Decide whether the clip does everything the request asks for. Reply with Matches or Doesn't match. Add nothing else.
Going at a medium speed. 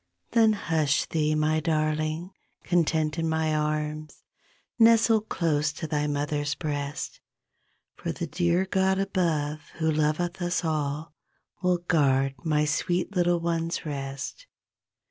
Doesn't match